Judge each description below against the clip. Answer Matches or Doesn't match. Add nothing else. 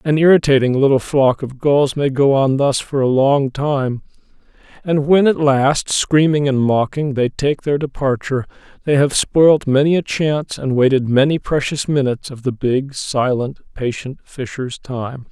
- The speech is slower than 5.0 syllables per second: Matches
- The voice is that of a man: Matches